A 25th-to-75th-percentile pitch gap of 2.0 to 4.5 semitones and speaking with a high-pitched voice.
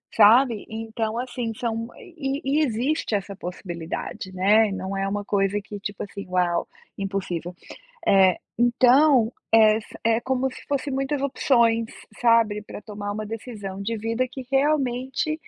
Yes: average, 4.1 semitones; high, 225 Hz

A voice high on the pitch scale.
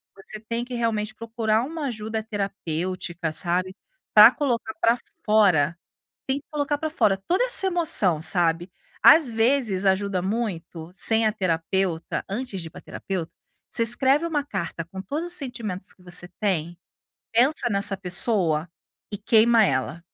Yes: high, 210 Hz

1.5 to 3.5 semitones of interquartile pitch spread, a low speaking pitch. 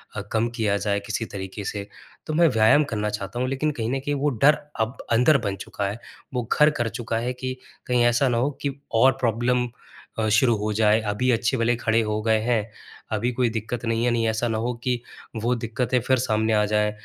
Yes: narrow, 2.4 semitones; low, 115 Hz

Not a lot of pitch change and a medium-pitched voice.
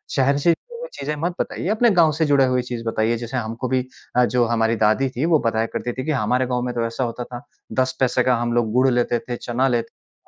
No: narrow, 2.3 semitones; low, 125 Hz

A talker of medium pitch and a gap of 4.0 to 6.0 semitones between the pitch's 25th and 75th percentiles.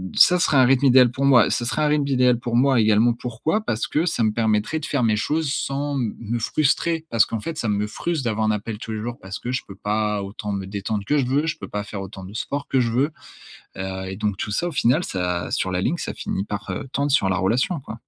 No: low, 115 Hz; average, 5.0 semitones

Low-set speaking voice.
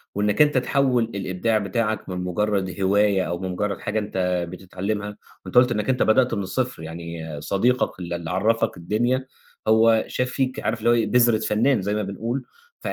Yes: low, 105 Hz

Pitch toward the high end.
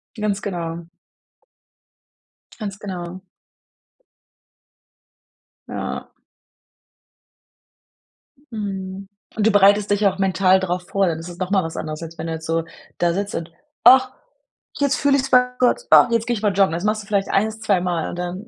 Yes: high, 195 Hz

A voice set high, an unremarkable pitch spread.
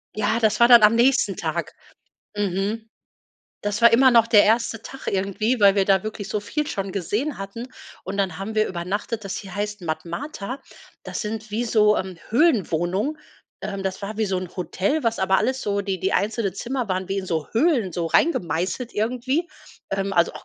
Yes: high, 205 Hz; average, 3.3 semitones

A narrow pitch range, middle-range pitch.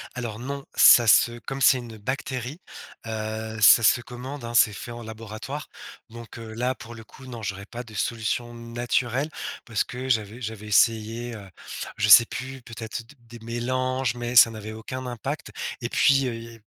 No: narrow, 2.2 semitones; low, 120 Hz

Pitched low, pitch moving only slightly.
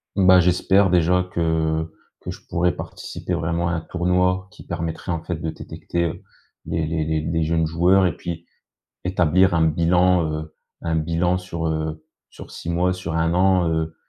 Yes: very low, 85 Hz; narrow, 1.9 semitones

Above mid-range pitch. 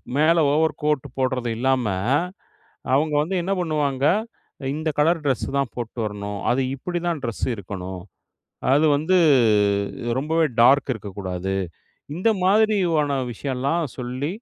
No: medium, 140 Hz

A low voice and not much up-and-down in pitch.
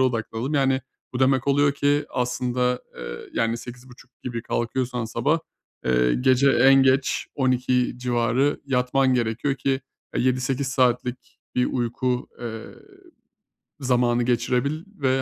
Yes: low, 125 Hz; narrow, 1.7 semitones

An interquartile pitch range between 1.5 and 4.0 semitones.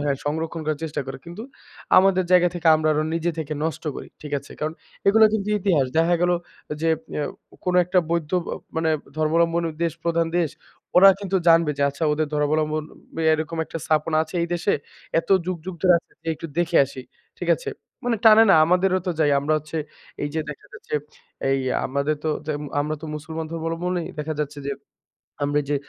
Yes: narrow, 2.5 semitones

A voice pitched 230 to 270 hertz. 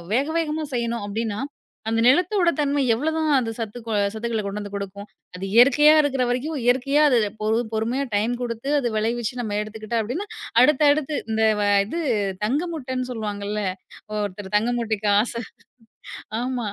Yes: high, 240 Hz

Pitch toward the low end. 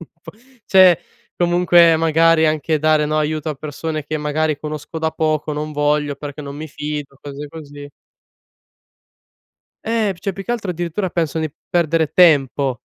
No: medium, 155 Hz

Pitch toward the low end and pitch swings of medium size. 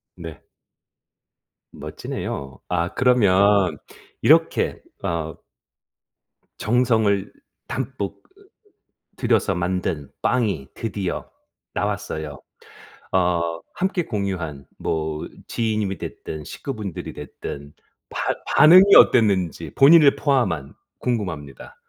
No: very low, 95 Hz; wide, 5.9 semitones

